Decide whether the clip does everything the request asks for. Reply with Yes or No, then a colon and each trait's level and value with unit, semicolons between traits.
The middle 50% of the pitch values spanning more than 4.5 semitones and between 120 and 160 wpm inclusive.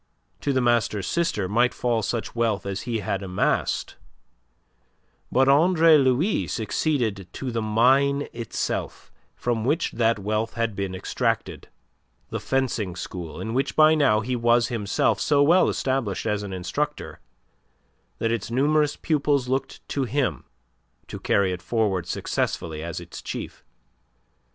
Yes: average, 4.9 semitones; average, 140 wpm